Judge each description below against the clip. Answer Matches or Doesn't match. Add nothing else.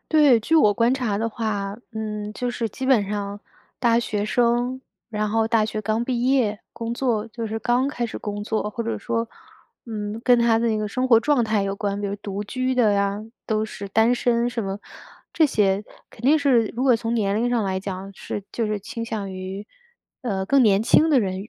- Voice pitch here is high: Matches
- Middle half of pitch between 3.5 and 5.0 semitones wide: Doesn't match